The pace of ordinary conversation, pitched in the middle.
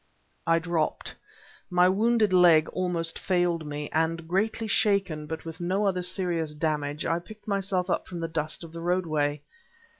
Yes: average, 160 wpm; medium, 170 Hz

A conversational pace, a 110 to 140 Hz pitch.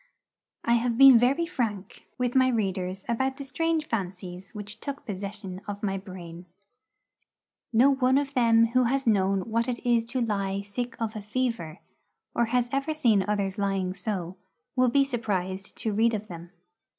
No: average, 170 wpm; high, 225 Hz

